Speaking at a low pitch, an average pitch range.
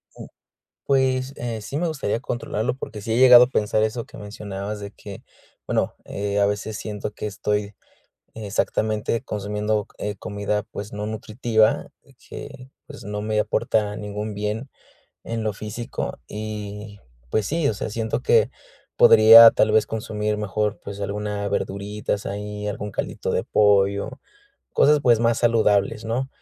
No: low, 105 Hz; narrow, 1.7 semitones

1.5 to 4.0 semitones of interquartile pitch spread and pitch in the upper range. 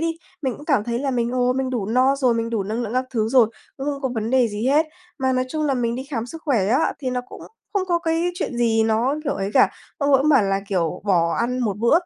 Yes: average, 3.6 semitones; very high, 250 Hz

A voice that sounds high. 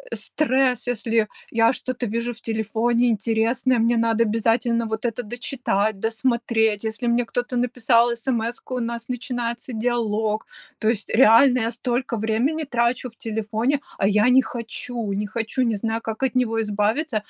Yes: high, 230 Hz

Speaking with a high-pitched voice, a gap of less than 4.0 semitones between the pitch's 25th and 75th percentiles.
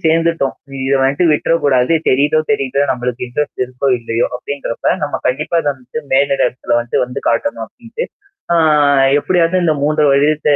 No: medium, 140 Hz; average, 3.5 semitones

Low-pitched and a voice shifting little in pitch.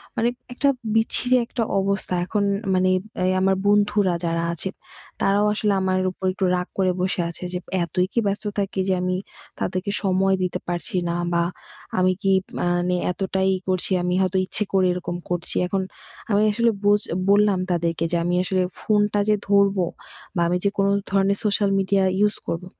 No: high, 190 Hz; narrow, 2.0 semitones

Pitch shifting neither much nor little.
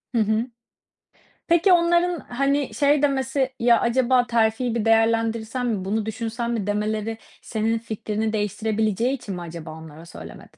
Yes: average, 3.1 semitones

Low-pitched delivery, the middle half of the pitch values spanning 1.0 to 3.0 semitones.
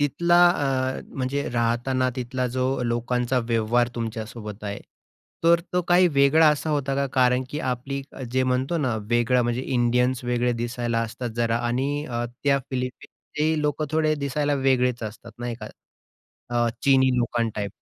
Yes: low, 125 Hz; average, 2.7 semitones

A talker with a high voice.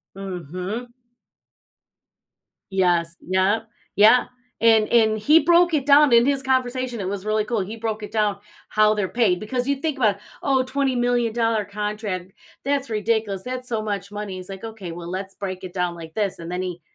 Yes: high, 215 Hz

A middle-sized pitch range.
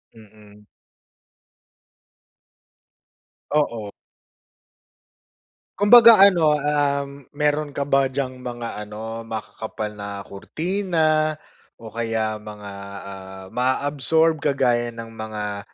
No: wide, 5.7 semitones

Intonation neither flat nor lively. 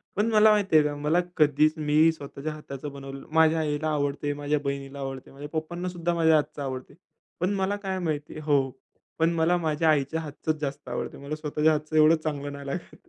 No: narrow, 2.1 semitones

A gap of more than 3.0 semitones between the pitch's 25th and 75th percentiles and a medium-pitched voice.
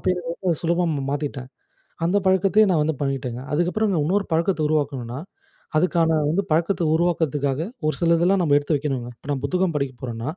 Yes: average, 3.9 semitones; medium, 160 Hz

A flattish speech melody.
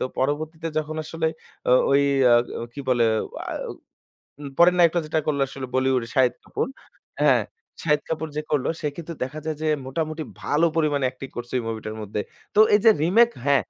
No: average, 3.5 semitones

